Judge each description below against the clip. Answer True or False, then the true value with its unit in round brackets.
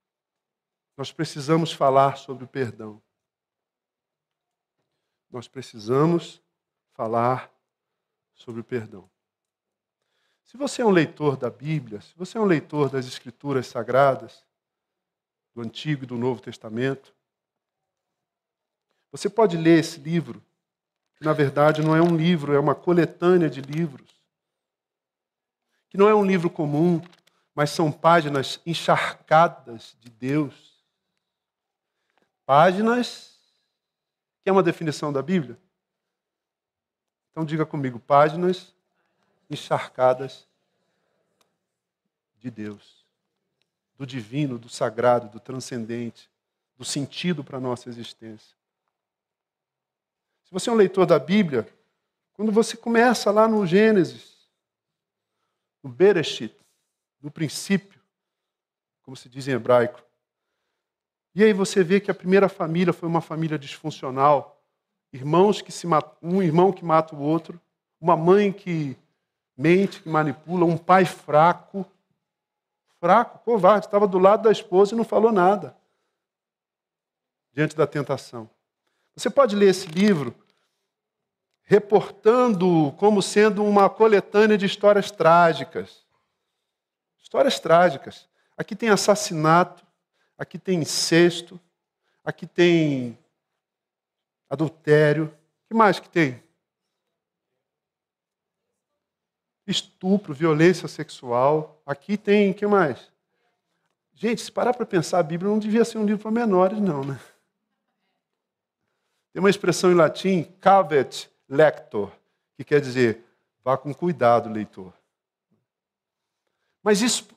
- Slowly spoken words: True (115 wpm)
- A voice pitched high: False (165 Hz)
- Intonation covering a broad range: True (5.7 semitones)